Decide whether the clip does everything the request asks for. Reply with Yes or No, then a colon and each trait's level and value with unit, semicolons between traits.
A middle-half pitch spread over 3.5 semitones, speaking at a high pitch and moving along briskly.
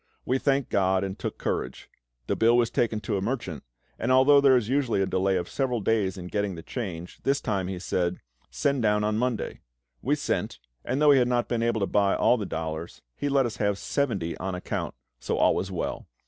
No: average, 4.9 semitones; low, 105 Hz; fast, 220 wpm